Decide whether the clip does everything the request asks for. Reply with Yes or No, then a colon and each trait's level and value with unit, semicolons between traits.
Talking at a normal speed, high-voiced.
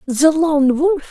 Yes: average, 165 wpm; very high, 300 Hz